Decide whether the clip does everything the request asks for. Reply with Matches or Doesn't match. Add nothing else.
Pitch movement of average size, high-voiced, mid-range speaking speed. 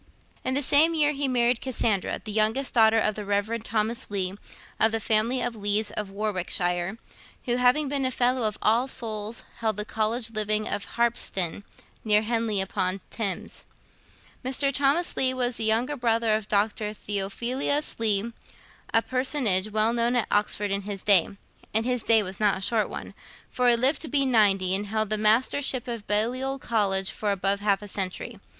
Matches